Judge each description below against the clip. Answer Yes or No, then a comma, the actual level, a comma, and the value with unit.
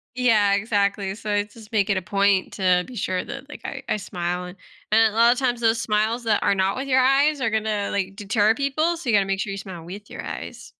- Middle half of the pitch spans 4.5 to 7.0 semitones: No, average, 3.4 semitones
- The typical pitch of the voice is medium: No, high, 210 Hz